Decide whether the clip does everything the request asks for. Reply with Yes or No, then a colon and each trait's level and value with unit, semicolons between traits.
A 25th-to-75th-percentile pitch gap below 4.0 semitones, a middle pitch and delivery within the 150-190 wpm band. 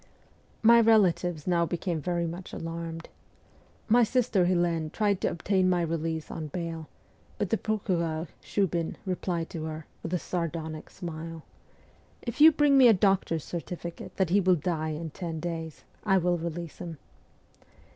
Yes: narrow, 2.6 semitones; medium, 170 Hz; average, 155 wpm